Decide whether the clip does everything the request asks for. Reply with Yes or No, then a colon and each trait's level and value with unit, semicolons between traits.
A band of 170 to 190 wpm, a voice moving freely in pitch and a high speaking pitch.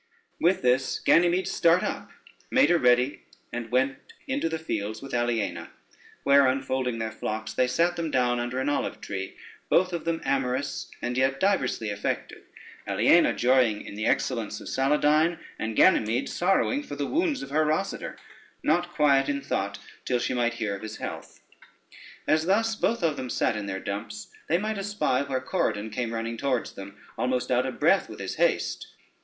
No: average, 180 wpm; wide, 6.0 semitones; low, 130 Hz